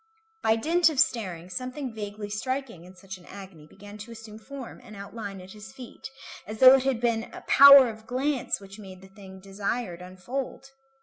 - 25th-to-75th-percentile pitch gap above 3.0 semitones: Yes, average, 4.7 semitones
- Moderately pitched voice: No, high, 215 Hz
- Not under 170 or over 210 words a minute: Yes, average, 190 wpm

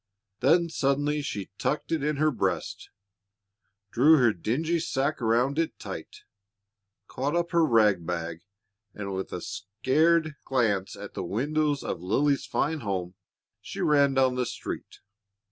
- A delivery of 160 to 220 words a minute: No, average, 145 wpm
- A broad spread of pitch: Yes, wide, 6.6 semitones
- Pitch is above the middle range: No, low, 135 Hz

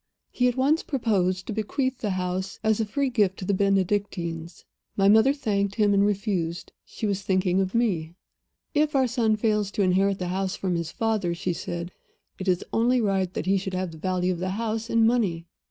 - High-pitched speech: Yes, high, 200 Hz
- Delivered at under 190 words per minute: No, fast, 205 wpm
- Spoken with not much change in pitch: No, average, 3.3 semitones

